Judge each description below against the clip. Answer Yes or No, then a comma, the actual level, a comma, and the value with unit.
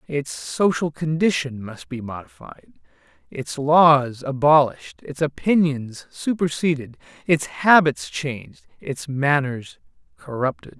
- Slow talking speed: Yes, slow, 100 wpm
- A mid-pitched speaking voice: Yes, medium, 145 Hz